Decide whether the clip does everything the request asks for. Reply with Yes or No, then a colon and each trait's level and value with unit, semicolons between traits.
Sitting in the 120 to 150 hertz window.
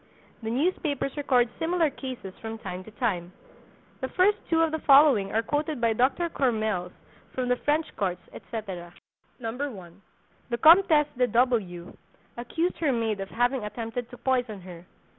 No: high, 245 Hz